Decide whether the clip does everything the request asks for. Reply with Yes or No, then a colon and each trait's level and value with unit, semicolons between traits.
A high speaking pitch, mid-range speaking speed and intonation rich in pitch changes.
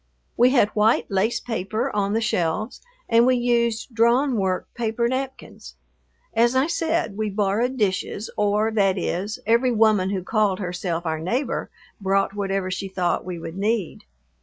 No: high, 215 Hz; average, 160 wpm; average, 3.6 semitones